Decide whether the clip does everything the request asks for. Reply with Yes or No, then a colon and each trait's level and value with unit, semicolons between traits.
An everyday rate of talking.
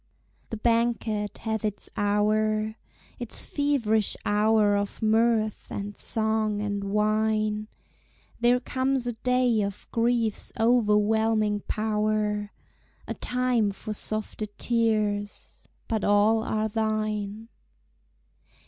No: slow, 100 wpm